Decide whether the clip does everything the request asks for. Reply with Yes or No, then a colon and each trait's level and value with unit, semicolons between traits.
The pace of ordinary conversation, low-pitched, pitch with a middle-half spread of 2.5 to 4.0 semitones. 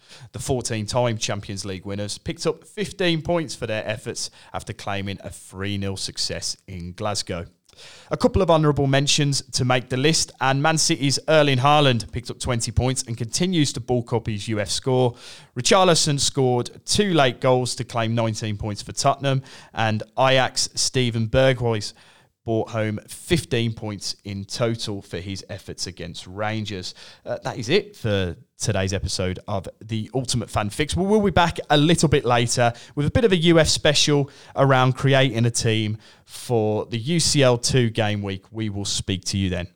No: average, 170 wpm; low, 120 Hz; average, 4.6 semitones